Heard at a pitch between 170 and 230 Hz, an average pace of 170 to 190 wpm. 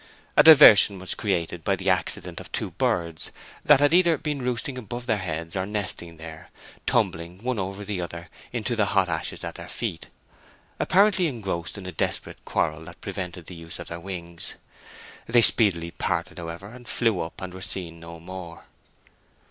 No: very low, 95 Hz; average, 180 wpm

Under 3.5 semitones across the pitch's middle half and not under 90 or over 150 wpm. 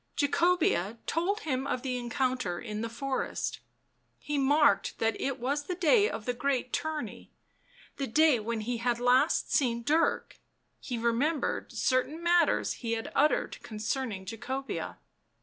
No: average, 4.3 semitones; average, 145 wpm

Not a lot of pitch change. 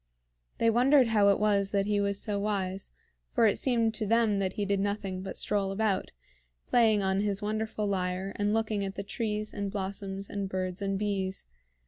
Yes: narrow, 1.5 semitones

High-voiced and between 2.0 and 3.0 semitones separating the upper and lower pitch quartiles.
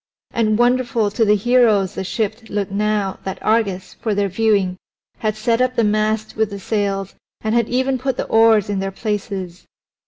Yes: high, 215 Hz; narrow, 2.4 semitones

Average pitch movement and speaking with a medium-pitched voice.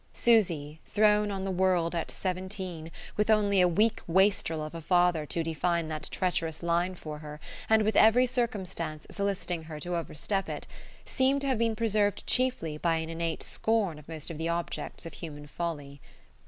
Yes: average, 4.4 semitones; medium, 175 Hz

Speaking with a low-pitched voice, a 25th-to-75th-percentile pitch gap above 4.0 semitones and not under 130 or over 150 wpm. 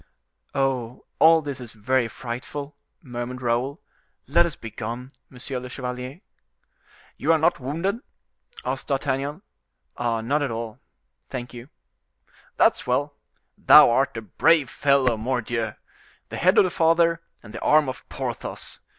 No: low, 130 Hz; average, 3.6 semitones; slow, 135 wpm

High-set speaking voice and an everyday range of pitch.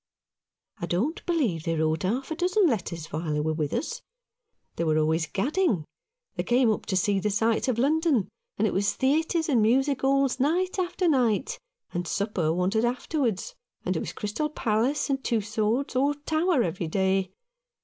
No: high, 230 Hz; wide, 7.6 semitones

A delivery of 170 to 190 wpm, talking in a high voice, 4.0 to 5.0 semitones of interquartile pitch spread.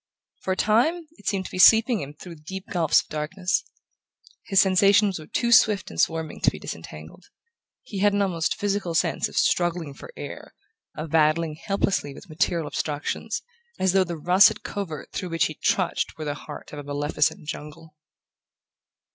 No: average, 175 wpm; medium, 175 Hz; average, 4.3 semitones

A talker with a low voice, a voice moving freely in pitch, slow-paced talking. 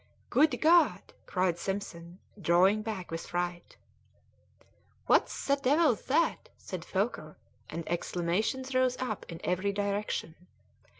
No: high, 200 Hz; wide, 6.6 semitones; slow, 115 wpm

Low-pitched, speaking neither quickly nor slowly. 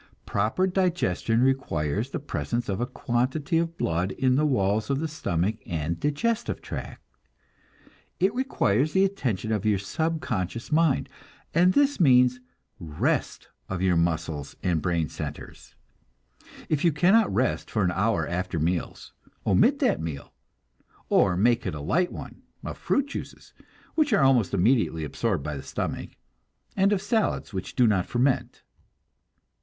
Yes: low, 120 Hz; average, 145 wpm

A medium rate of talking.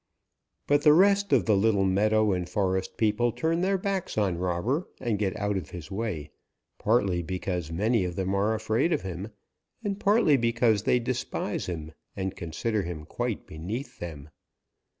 Yes: average, 170 wpm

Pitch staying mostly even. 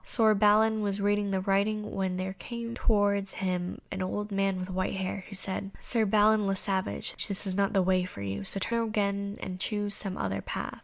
Yes: narrow, 1.8 semitones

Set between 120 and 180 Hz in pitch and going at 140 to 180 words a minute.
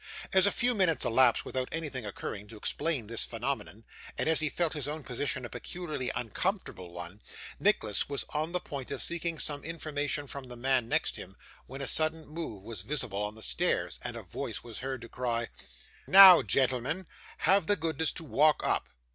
No: medium, 140 Hz; average, 190 wpm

